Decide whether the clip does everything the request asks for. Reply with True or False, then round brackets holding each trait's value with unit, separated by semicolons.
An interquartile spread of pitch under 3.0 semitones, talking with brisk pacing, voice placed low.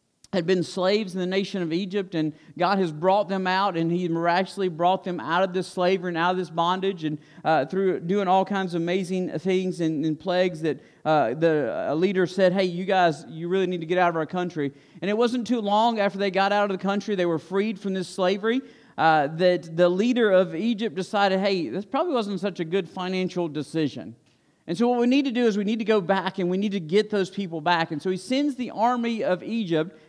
False (2.6 semitones; 240 wpm; 185 Hz)